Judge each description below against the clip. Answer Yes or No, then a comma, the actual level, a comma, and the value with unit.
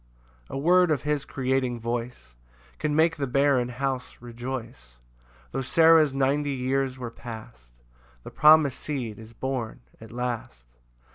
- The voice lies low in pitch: Yes, low, 130 Hz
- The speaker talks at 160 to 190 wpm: No, average, 140 wpm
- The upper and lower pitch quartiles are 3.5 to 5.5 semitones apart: No, average, 3.1 semitones